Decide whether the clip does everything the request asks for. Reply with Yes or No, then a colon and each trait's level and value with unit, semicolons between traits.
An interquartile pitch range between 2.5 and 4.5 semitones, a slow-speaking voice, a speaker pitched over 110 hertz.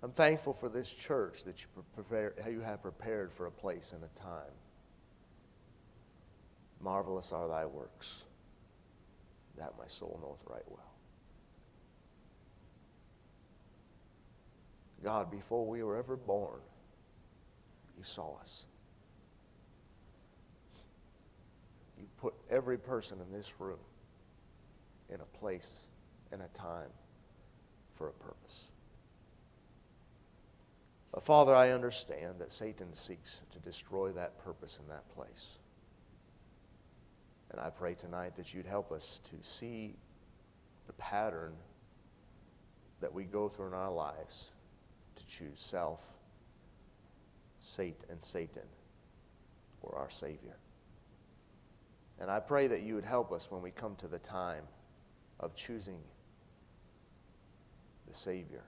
No: average, 4.2 semitones; slow, 110 wpm; low, 100 Hz